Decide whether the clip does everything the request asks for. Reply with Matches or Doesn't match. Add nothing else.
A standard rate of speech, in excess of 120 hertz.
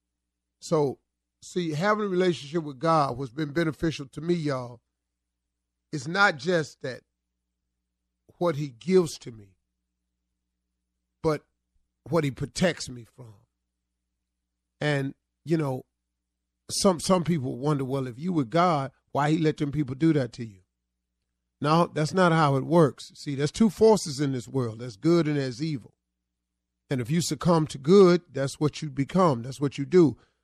Matches